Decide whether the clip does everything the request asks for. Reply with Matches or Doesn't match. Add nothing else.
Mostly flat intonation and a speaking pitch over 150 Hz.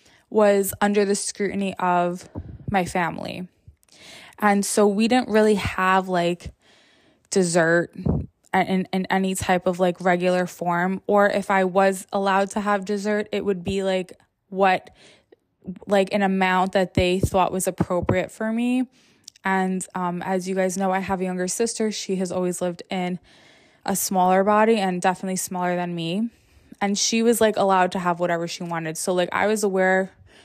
Matches